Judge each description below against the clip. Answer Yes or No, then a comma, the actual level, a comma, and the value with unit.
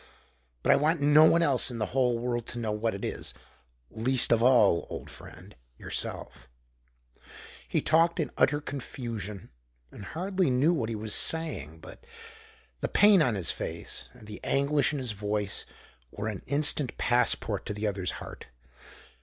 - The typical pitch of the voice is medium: No, low, 120 Hz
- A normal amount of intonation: No, wide, 5.8 semitones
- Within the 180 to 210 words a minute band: No, average, 165 wpm